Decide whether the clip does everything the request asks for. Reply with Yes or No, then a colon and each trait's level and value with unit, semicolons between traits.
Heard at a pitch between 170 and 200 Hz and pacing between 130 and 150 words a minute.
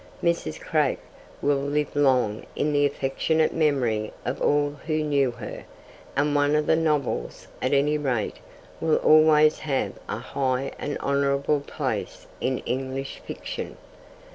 No: medium, 145 Hz; average, 140 wpm